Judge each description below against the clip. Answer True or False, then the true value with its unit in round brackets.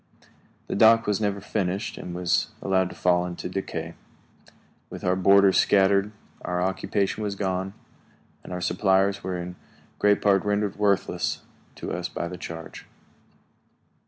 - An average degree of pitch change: False (2.0 semitones)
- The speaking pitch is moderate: False (95 Hz)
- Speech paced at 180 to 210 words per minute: False (145 wpm)